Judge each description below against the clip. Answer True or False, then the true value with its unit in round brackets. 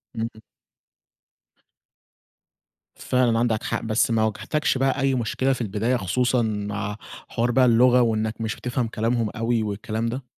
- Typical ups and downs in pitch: False (2.3 semitones)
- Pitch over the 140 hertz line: False (115 Hz)